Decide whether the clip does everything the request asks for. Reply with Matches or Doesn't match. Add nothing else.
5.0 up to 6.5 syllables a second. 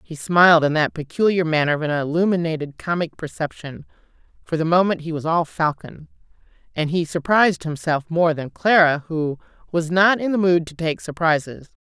Matches